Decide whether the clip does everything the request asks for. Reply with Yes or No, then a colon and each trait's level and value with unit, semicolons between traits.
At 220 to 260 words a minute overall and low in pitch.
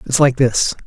No: fast, 210 wpm; low, 125 Hz